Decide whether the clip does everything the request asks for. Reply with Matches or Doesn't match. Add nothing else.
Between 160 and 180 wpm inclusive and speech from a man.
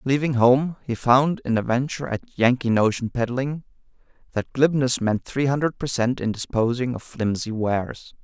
Matches